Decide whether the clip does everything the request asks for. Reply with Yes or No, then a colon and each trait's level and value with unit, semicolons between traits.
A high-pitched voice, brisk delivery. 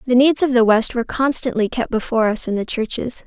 Yes: high, 240 Hz; fast, 240 wpm